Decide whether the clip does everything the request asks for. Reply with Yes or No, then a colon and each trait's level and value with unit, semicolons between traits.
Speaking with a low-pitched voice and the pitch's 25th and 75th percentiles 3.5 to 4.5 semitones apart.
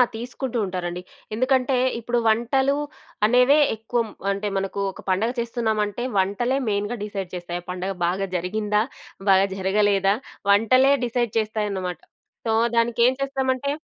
No: high, 215 Hz; average, 3.8 semitones